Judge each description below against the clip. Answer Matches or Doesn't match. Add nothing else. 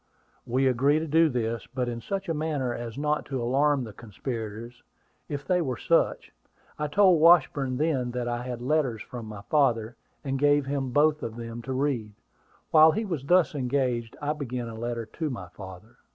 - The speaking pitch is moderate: Doesn't match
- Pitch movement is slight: Doesn't match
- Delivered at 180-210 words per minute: Matches